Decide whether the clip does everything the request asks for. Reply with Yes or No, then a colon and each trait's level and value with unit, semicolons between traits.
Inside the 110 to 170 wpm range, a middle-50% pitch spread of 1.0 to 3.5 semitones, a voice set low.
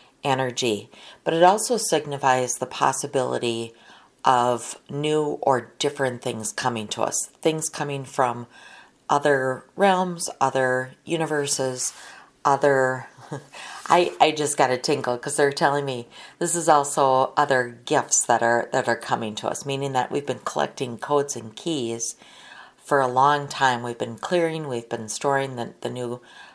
Yes: average, 150 wpm; average, 3.2 semitones; low, 130 Hz